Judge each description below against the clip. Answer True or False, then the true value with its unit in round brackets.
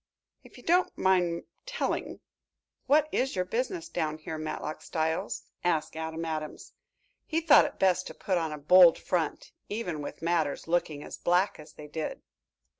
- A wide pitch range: False (3.5 semitones)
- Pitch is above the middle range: False (170 Hz)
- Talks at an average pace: True (165 wpm)